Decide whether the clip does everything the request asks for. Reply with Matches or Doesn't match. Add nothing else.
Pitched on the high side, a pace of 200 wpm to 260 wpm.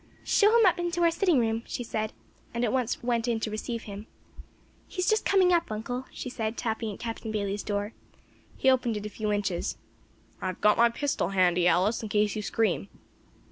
Matches